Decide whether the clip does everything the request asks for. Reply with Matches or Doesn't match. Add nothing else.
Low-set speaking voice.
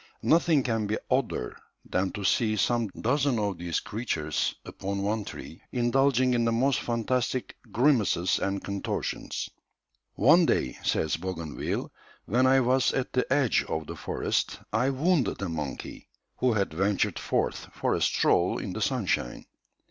Matches